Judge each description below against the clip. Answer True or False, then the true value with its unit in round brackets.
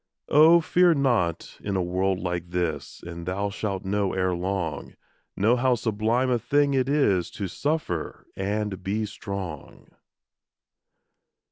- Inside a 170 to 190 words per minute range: False (135 wpm)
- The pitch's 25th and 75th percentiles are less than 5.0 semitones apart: False (5.4 semitones)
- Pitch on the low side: True (100 Hz)